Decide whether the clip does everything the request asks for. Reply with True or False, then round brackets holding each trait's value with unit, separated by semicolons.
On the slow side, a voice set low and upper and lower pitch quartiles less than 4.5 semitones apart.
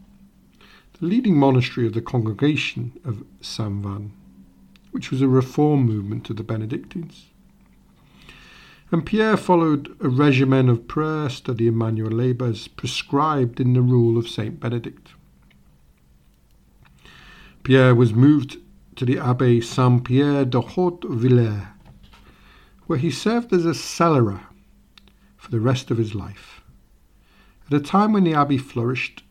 False (130 wpm; 125 Hz; 4.8 semitones)